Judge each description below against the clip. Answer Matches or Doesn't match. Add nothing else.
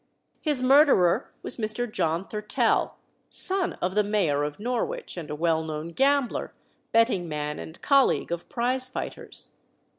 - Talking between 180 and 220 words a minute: Doesn't match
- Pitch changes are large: Matches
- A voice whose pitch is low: Doesn't match